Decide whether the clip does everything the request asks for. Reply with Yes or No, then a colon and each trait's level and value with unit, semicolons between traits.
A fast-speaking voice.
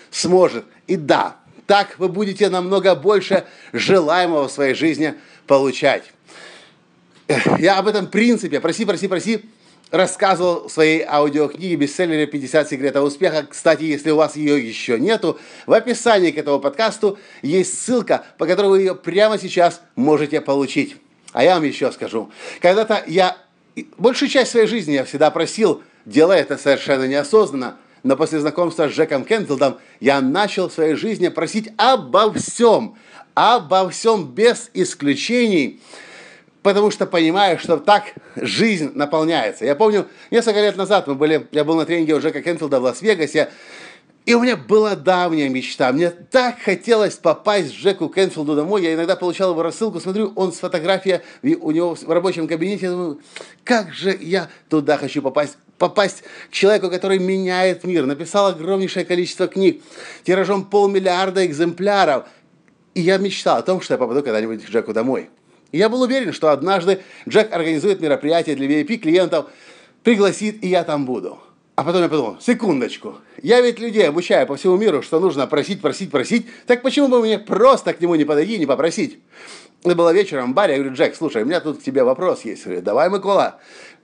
Yes: fast, 165 wpm